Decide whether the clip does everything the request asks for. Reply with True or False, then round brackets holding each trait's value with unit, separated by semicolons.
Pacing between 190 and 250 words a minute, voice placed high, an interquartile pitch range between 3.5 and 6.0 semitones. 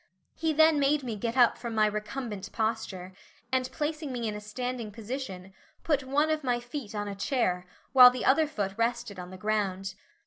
True (195 wpm; 235 Hz; 4.5 semitones)